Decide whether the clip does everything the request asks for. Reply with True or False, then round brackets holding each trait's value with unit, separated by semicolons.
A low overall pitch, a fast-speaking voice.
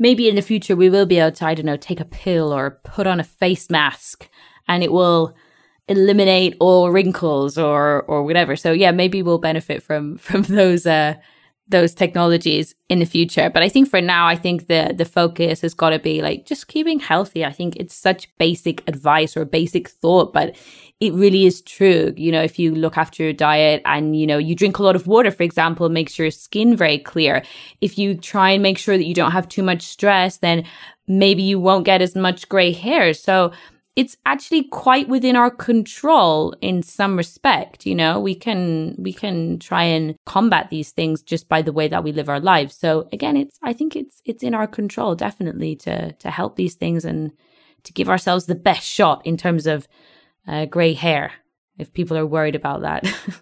False (170 Hz; 210 wpm)